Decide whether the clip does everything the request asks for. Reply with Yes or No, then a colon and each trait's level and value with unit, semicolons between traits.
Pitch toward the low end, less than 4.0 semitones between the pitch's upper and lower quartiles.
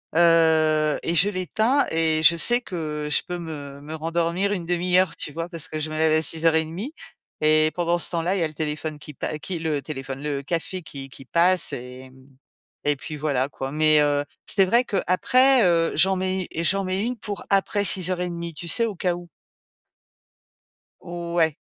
No: medium, 165 Hz; average, 3.1 semitones